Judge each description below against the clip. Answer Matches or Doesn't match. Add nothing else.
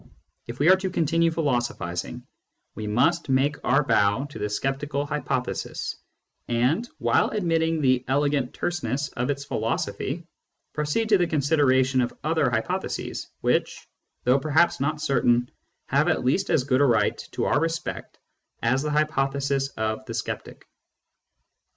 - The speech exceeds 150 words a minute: Doesn't match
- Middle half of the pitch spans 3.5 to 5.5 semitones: Matches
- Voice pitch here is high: Doesn't match